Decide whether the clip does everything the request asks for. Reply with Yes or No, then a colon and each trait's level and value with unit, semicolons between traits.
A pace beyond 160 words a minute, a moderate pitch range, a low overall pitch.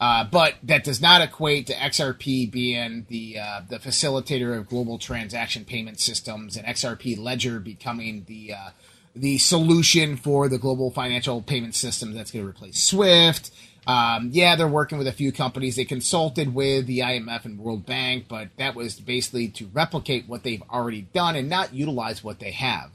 Yes: average, 180 wpm; average, 3.3 semitones; low, 125 Hz